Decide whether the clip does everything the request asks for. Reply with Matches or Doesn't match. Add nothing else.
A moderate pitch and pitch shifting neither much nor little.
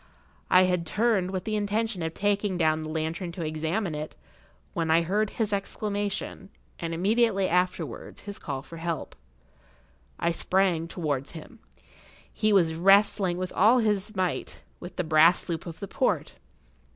Matches